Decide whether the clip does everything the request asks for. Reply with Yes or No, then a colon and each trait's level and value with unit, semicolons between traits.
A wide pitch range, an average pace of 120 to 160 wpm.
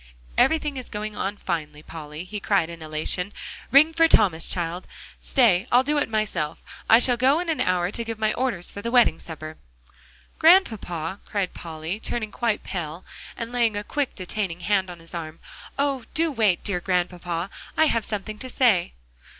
No: wide, 5.8 semitones; average, 180 wpm